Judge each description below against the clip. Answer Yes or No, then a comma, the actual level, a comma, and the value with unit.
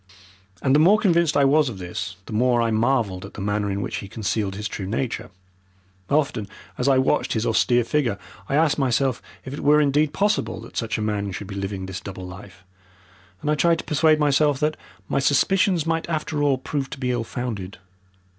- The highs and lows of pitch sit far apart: Yes, wide, 6.4 semitones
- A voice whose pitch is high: No, low, 125 Hz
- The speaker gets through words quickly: Yes, fast, 210 wpm